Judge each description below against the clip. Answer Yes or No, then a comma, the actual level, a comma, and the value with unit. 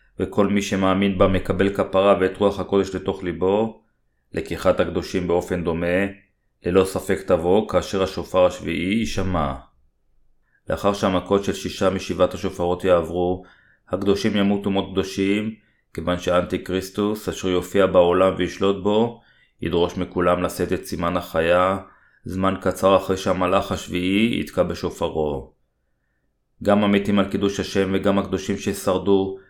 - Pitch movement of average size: No, narrow, 1.8 semitones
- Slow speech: No, average, 125 wpm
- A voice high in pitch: No, very low, 95 Hz